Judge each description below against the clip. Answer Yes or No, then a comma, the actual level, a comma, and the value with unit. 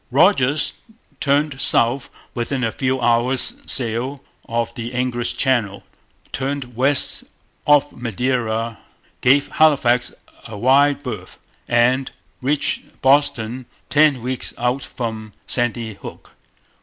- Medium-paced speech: No, slow, 105 wpm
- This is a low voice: Yes, low, 125 Hz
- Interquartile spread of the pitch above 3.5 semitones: No, average, 2.7 semitones